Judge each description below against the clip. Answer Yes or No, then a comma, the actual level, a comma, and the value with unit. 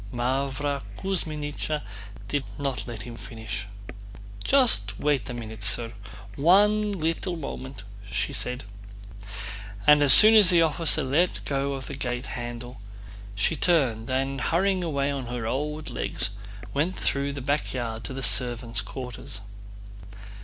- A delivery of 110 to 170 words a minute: Yes, average, 140 wpm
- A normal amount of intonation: Yes, average, 4.3 semitones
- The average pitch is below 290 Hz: Yes, low, 135 Hz